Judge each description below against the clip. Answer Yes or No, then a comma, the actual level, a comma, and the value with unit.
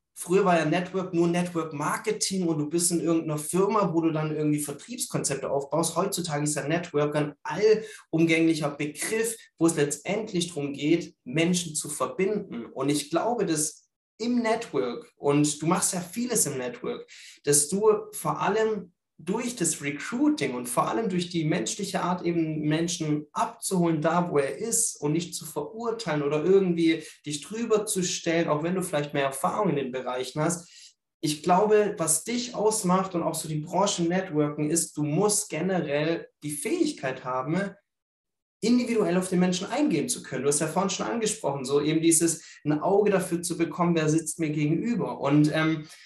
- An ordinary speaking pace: Yes, average, 170 wpm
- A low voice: No, medium, 165 Hz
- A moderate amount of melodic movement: Yes, average, 4.4 semitones